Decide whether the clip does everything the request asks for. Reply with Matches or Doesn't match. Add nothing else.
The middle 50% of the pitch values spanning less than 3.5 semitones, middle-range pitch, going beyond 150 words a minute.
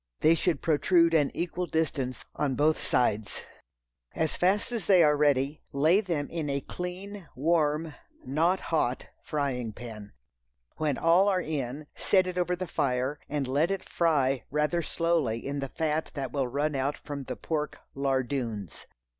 Doesn't match